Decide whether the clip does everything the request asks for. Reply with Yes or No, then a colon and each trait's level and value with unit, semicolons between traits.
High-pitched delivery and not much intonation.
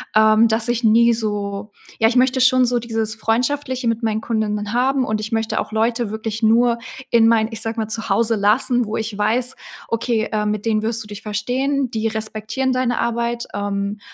Yes: high, 225 Hz; narrow, 1.8 semitones